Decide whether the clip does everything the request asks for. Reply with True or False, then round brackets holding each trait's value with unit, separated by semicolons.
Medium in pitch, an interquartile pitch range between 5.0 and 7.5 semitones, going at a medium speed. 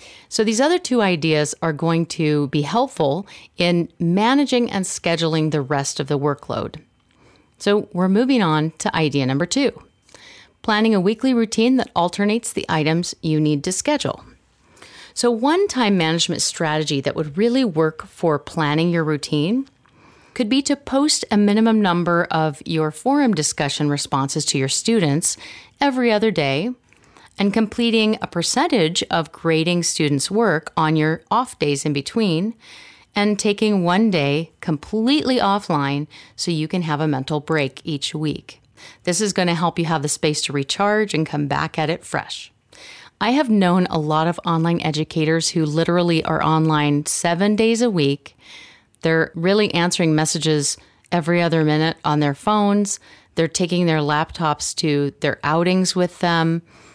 True (170 Hz; 5.6 semitones; 160 wpm)